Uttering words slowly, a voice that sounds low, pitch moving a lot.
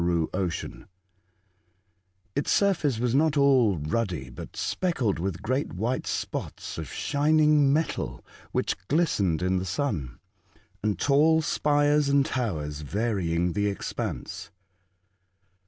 Yes: slow, 105 wpm; low, 120 Hz; wide, 8.2 semitones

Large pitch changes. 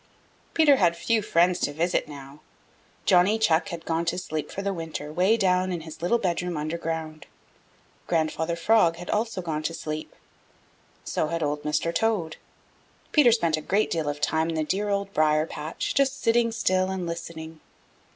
No: average, 3.9 semitones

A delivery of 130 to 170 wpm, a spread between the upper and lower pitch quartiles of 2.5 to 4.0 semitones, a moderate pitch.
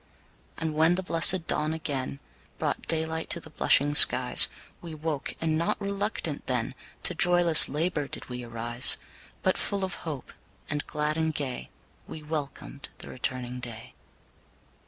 Yes: average, 150 wpm; average, 3.4 semitones; medium, 155 Hz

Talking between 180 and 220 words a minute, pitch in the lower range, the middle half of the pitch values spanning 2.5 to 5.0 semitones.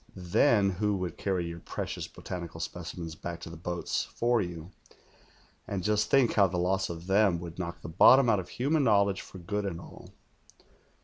Yes: average, 185 wpm; very low, 90 Hz; average, 3.2 semitones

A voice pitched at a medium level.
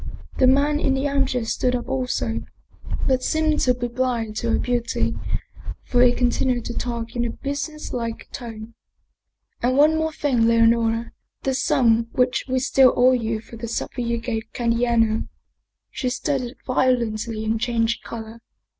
No: high, 240 Hz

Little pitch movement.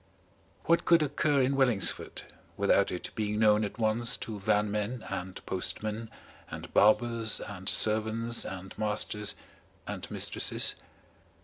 Yes: narrow, 2.3 semitones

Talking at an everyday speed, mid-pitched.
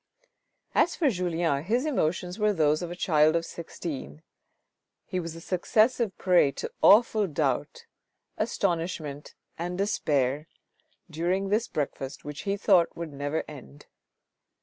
No: slow, 130 wpm; medium, 170 Hz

